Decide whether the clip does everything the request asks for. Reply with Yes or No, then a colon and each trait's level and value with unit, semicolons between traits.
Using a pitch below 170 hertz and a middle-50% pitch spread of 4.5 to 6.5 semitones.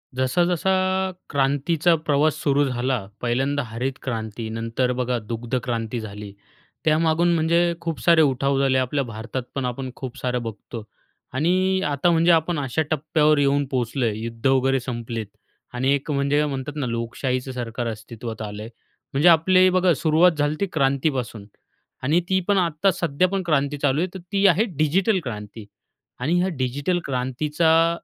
Yes: medium, 140 Hz; average, 4.9 semitones